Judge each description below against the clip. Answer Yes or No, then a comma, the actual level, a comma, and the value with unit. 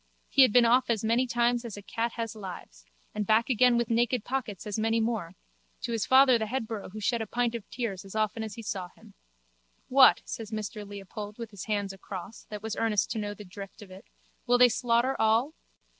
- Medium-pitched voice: No, high, 220 Hz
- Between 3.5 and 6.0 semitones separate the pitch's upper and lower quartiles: No, narrow, 2.5 semitones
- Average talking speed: No, fast, 220 wpm